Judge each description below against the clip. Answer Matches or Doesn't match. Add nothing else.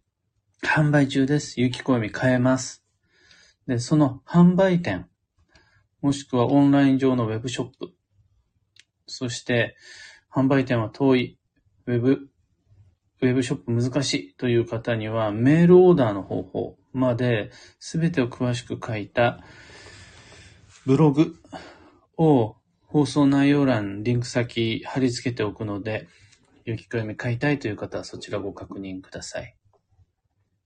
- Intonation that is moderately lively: Matches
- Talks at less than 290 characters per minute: Matches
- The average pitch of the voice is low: Matches